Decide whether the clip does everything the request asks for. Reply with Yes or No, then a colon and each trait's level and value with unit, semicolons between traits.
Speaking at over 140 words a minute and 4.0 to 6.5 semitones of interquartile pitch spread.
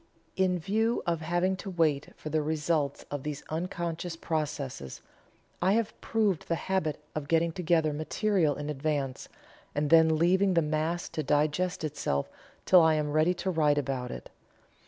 No: average, 160 wpm; average, 3.0 semitones